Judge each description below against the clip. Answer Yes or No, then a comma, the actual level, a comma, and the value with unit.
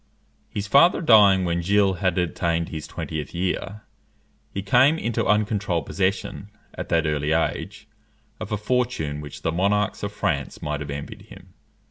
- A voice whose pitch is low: Yes, very low, 95 Hz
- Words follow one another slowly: No, average, 155 wpm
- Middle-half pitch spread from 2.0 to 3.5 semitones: No, average, 4.3 semitones